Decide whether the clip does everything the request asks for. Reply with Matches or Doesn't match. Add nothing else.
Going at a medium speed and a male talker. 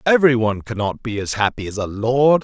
Doesn't match